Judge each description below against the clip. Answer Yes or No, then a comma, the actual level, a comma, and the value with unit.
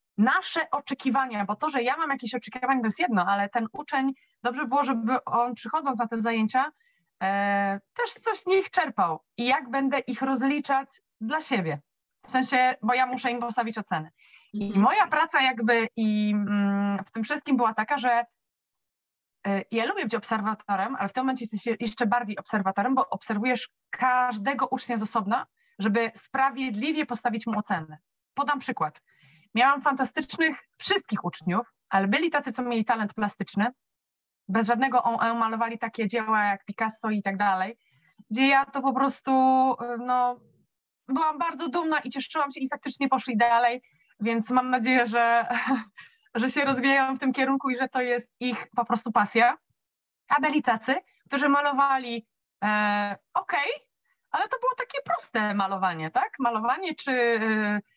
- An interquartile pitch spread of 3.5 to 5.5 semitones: Yes, average, 3.9 semitones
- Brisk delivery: Yes, fast, 165 wpm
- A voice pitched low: No, high, 245 Hz